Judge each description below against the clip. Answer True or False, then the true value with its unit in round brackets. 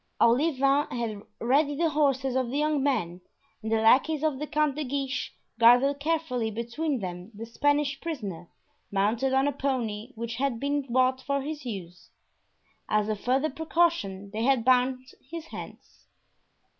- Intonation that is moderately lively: True (4.2 semitones)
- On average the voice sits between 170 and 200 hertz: False (260 Hz)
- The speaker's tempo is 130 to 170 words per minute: True (155 wpm)